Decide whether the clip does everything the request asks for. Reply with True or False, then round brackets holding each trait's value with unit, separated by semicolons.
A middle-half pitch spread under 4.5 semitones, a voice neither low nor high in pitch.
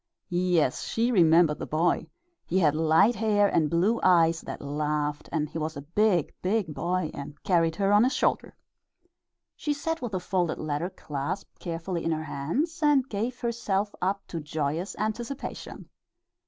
False (5.2 semitones; 175 Hz)